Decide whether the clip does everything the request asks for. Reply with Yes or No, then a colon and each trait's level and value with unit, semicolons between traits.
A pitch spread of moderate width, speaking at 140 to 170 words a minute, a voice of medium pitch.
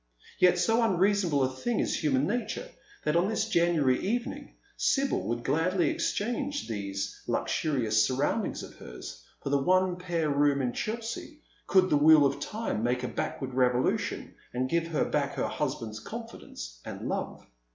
No: wide, 7.4 semitones; average, 160 wpm; medium, 150 Hz